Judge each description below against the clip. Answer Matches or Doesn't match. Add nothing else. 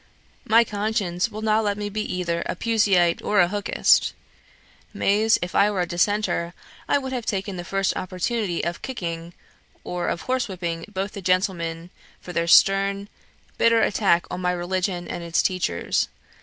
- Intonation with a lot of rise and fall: Doesn't match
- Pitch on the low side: Doesn't match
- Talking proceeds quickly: Doesn't match